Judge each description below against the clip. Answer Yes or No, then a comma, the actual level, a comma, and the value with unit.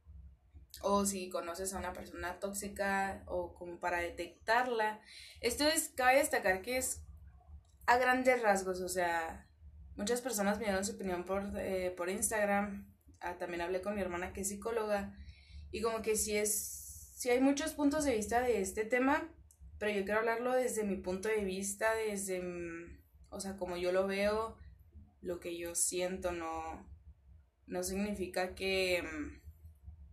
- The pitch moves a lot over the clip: No, average, 4.4 semitones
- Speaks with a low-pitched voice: No, high, 190 Hz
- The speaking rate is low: No, average, 165 wpm